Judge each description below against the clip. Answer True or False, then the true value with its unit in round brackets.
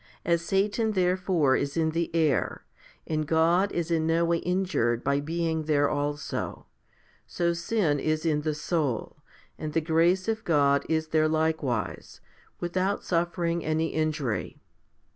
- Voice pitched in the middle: True (160 Hz)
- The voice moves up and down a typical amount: False (2.3 semitones)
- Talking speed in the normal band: True (145 wpm)